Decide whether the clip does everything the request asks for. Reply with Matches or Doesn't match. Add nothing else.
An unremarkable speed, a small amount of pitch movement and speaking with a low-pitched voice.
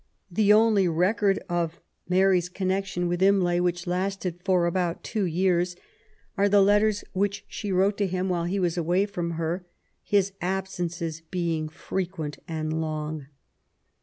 Doesn't match